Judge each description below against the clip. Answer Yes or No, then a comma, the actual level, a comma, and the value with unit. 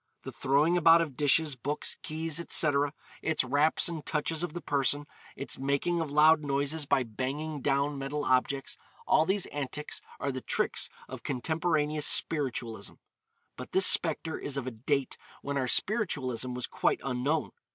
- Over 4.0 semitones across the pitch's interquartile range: No, average, 2.8 semitones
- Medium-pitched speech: Yes, medium, 145 Hz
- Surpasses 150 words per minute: Yes, average, 160 wpm